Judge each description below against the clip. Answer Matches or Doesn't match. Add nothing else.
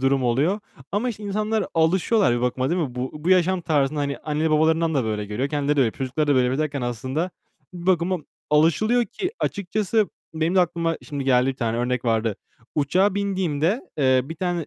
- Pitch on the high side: Doesn't match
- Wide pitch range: Matches